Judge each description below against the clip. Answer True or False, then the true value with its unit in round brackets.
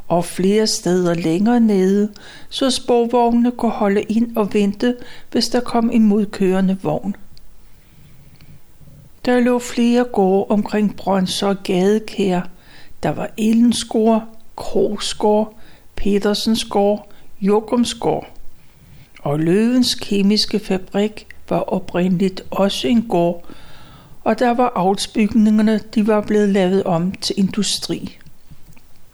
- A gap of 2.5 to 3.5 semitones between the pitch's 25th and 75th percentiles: True (3.0 semitones)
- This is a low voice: False (210 Hz)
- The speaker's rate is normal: False (105 wpm)